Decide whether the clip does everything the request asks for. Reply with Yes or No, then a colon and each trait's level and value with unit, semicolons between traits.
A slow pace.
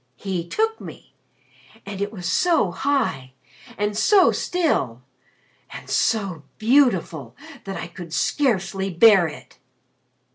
Yes: slow, 115 wpm